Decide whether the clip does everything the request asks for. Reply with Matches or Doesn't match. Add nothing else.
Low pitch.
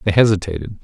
Matches